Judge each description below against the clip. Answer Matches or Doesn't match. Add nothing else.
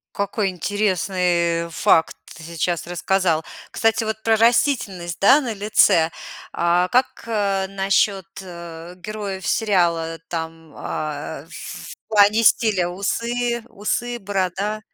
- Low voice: Doesn't match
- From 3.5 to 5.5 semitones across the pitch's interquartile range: Matches